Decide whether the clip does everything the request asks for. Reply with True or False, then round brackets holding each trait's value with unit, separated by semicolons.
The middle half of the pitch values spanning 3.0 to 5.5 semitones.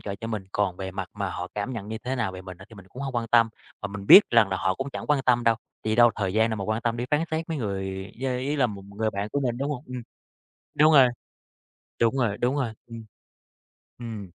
True (4.2 semitones)